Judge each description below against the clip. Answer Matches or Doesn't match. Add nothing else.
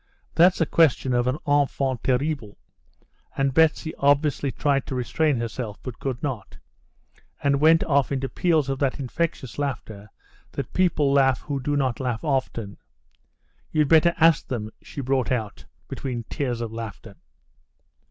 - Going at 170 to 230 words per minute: Doesn't match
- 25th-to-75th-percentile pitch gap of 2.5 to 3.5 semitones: Matches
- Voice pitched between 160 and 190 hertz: Doesn't match